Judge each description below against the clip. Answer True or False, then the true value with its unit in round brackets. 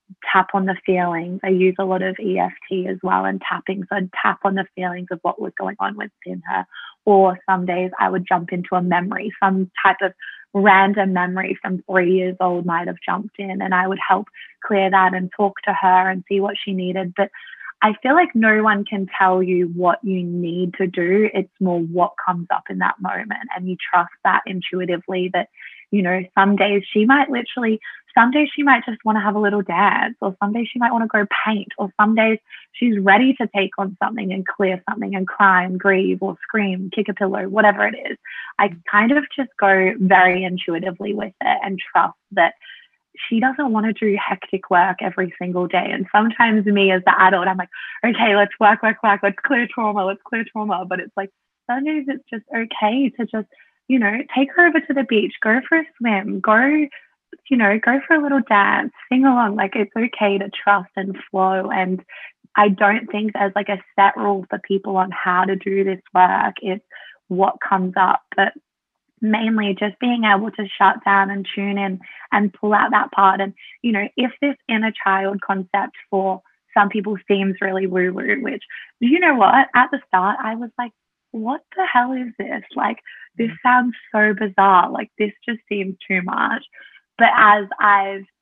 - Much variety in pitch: False (2.9 semitones)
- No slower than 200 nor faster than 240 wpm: True (205 wpm)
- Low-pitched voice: False (200 Hz)